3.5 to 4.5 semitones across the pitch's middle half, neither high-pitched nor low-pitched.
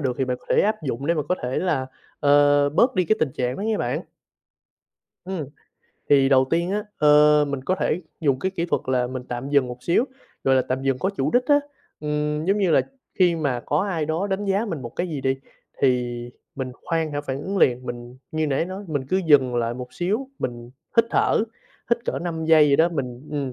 No: average, 5.3 semitones; medium, 150 Hz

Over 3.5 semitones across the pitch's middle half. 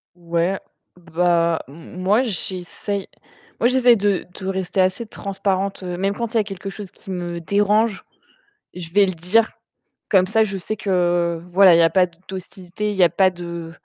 No: narrow, 2.5 semitones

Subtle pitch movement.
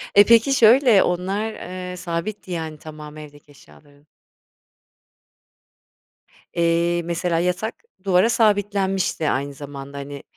No: average, 5.2 semitones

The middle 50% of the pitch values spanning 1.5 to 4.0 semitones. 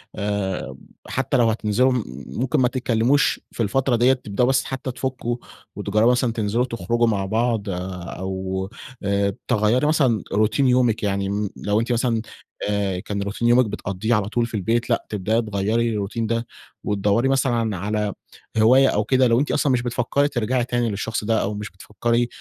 Yes: average, 3.3 semitones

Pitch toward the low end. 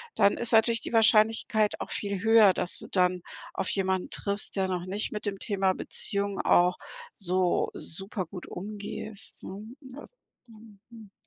No: high, 200 Hz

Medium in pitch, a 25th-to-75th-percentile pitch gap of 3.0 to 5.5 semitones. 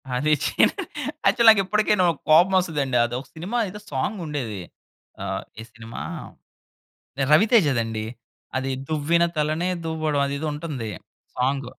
Yes: medium, 150 Hz; average, 5.1 semitones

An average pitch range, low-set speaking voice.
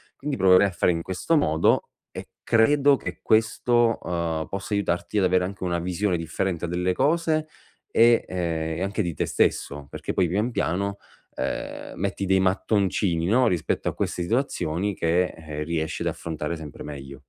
Yes: average, 4.4 semitones; very low, 90 Hz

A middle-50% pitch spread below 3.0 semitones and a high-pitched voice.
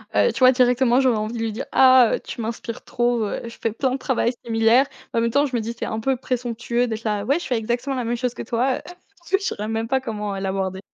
Yes: narrow, 2.4 semitones; high, 235 Hz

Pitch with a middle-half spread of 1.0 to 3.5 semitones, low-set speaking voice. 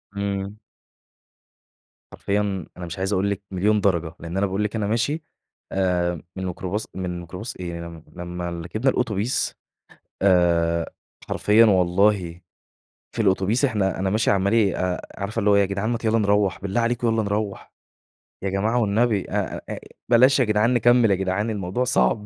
Yes: average, 3.1 semitones; low, 100 Hz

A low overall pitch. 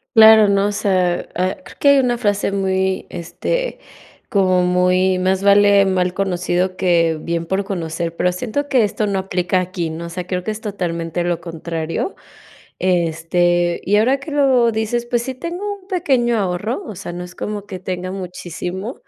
No: high, 190 Hz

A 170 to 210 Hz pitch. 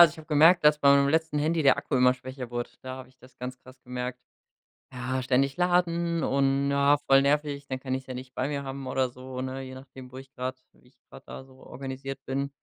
No: low, 135 Hz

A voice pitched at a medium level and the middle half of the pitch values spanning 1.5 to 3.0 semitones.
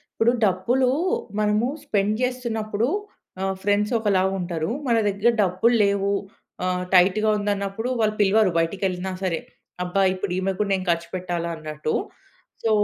No: high, 200 Hz; average, 2.7 semitones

